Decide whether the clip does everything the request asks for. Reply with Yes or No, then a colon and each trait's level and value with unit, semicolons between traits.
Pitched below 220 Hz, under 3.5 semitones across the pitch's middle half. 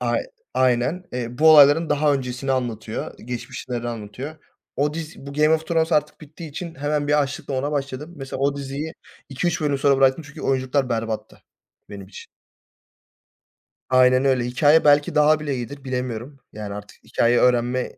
Yes: medium, 140 Hz; average, 3.1 semitones